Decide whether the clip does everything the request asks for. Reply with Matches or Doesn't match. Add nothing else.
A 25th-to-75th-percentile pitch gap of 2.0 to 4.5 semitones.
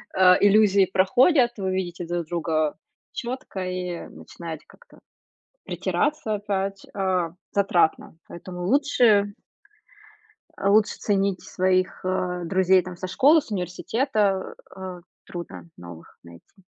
Matches